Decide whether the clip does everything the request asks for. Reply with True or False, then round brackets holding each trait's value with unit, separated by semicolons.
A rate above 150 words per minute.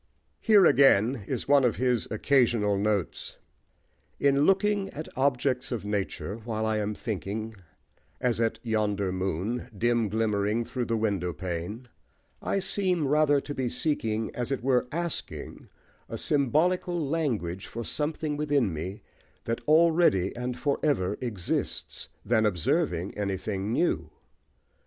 False (135 wpm)